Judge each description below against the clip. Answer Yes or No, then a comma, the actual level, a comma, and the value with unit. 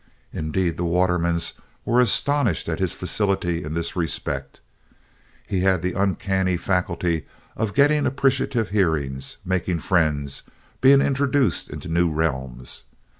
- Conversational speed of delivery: No, slow, 125 wpm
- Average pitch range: Yes, average, 4.1 semitones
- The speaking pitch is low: Yes, very low, 90 Hz